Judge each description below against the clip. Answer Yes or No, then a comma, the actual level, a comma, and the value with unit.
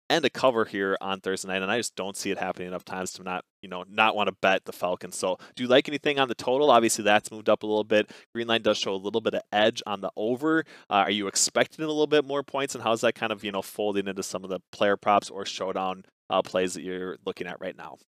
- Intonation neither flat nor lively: Yes, average, 3.6 semitones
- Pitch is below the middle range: Yes, low, 105 Hz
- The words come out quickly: Yes, fast, 285 wpm